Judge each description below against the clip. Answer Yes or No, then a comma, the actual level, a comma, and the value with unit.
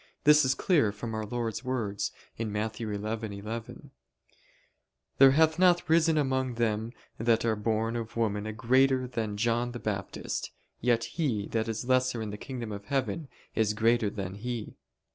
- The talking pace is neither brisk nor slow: Yes, average, 160 wpm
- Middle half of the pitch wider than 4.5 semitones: No, average, 3.2 semitones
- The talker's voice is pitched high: No, low, 115 Hz